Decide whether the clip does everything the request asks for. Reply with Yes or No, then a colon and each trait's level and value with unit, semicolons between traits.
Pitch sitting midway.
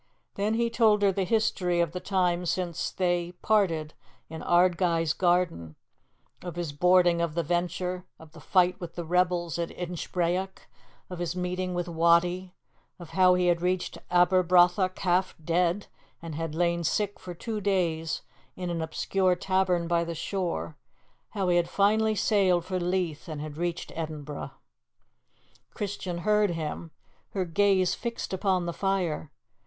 Yes: medium, 180 Hz